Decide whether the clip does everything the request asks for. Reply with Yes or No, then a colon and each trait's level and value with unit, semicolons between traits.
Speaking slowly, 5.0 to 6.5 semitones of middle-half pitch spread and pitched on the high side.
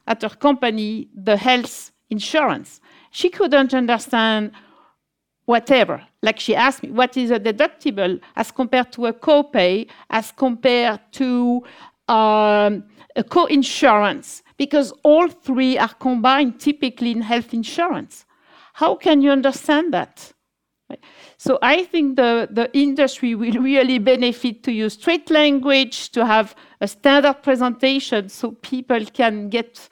No: slow, 130 wpm; average, 3.8 semitones; very high, 255 Hz